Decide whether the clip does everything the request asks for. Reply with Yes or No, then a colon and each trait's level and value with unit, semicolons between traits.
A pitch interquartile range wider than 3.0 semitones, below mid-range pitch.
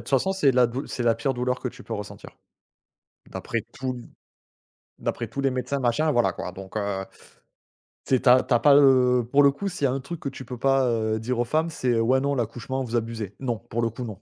No: average, 2.7 semitones; low, 125 Hz